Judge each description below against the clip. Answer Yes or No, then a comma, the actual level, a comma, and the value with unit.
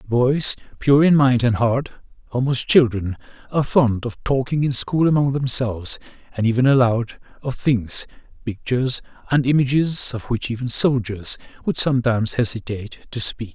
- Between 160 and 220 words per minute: No, average, 145 wpm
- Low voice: Yes, low, 125 Hz